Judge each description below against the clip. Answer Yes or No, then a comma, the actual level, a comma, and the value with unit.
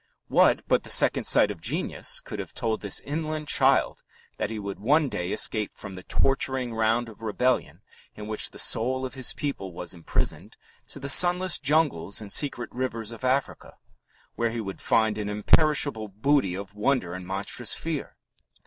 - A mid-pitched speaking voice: No, low, 115 Hz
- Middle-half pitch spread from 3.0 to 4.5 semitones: No, average, 5.0 semitones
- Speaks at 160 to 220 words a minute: Yes, average, 175 wpm